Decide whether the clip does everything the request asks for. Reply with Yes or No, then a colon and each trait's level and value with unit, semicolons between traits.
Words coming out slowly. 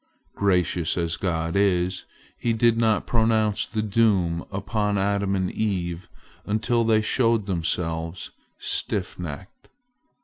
Yes: slow, 115 wpm